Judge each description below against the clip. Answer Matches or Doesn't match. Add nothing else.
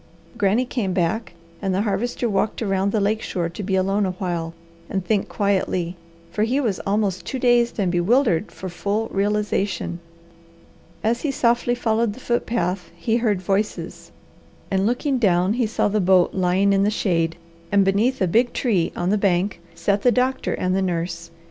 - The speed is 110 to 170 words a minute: Doesn't match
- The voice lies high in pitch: Matches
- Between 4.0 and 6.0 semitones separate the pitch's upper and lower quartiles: Doesn't match